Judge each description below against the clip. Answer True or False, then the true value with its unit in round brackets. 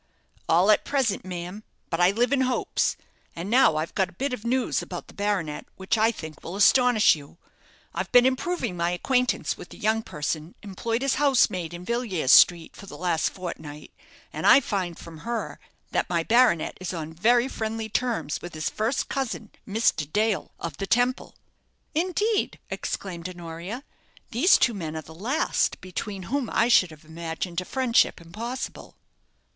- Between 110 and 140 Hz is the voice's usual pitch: False (200 Hz)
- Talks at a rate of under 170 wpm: False (175 wpm)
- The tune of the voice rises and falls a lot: True (6.2 semitones)